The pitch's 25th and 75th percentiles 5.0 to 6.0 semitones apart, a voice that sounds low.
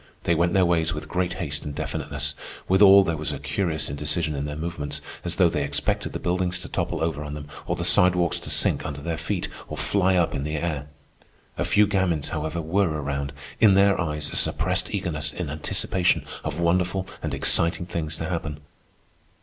No: average, 3.2 semitones; very low, 85 Hz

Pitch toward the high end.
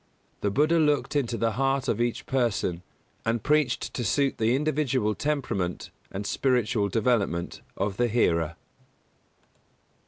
No: low, 120 Hz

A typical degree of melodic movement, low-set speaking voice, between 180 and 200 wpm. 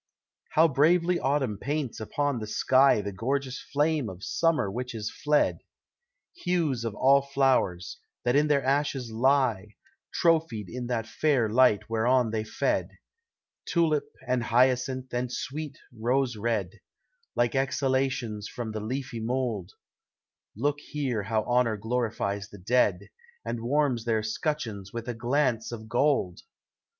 No: average, 4.0 semitones; low, 125 Hz; slow, 135 wpm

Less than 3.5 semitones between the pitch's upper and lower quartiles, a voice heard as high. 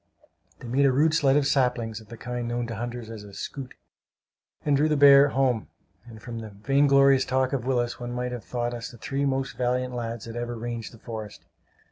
No: average, 2.7 semitones; low, 125 Hz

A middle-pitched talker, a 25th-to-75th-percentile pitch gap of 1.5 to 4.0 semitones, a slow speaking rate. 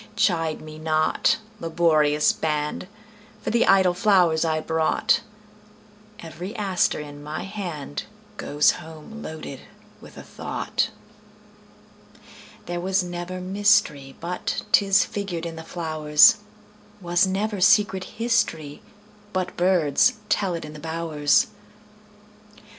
No: medium, 175 Hz; average, 4.7 semitones; slow, 95 wpm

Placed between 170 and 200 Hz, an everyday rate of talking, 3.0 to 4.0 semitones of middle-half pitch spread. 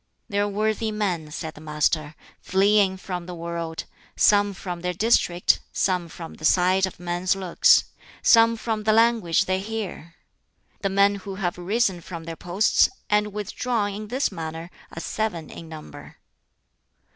Yes: high, 190 Hz; average, 155 wpm; average, 3.6 semitones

